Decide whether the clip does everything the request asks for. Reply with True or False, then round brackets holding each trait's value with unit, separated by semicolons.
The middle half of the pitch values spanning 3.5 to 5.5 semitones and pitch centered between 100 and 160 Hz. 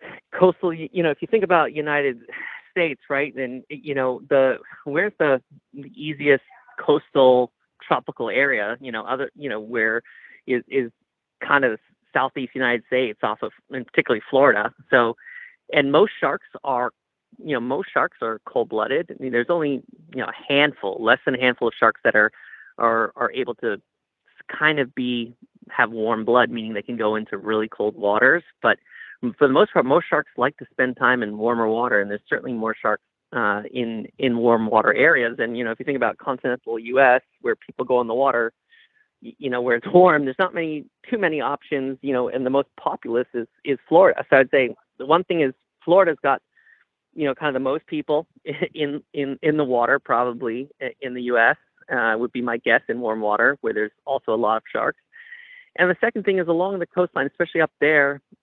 True (4.2 semitones; 135 Hz)